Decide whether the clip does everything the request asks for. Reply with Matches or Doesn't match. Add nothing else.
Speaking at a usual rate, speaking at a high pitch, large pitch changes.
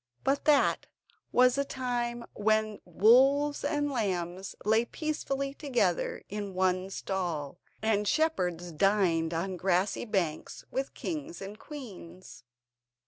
Doesn't match